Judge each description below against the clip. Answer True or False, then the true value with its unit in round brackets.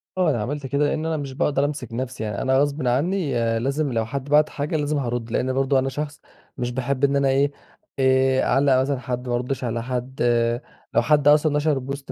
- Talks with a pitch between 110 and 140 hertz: True (135 Hz)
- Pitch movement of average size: False (2.3 semitones)